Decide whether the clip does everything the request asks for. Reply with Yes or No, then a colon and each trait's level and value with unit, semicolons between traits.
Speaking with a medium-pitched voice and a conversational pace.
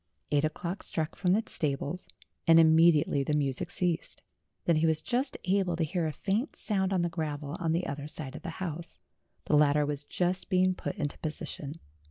Yes: medium, 165 Hz; average, 195 wpm